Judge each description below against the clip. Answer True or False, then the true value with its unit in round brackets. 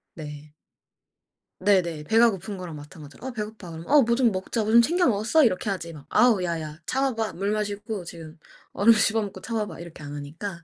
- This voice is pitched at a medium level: False (200 Hz)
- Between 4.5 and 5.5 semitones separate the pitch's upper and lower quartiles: True (5.2 semitones)